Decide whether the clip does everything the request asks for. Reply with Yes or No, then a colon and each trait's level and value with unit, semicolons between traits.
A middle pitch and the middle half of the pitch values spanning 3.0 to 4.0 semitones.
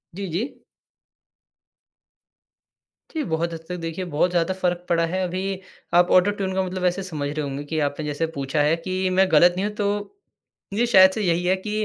No: medium, 180 Hz; narrow, 2.5 semitones